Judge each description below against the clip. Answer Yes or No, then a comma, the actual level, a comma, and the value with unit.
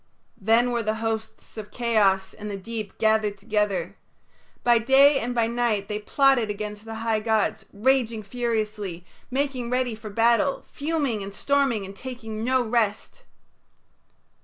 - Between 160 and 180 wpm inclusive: No, average, 145 wpm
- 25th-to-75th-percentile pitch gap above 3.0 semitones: No, narrow, 2.6 semitones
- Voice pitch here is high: Yes, high, 225 Hz